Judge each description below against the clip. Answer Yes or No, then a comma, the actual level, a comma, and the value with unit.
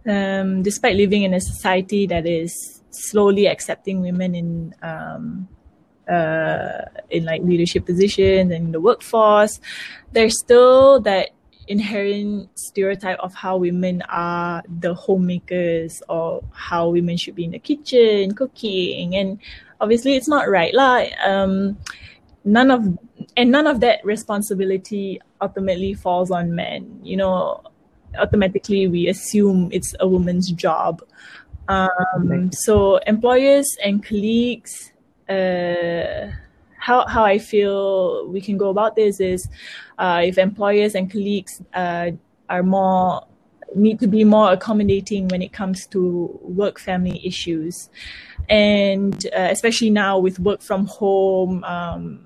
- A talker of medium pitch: No, high, 195 Hz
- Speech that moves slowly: Yes, slow, 130 wpm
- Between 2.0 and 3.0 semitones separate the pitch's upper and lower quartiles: Yes, narrow, 2.5 semitones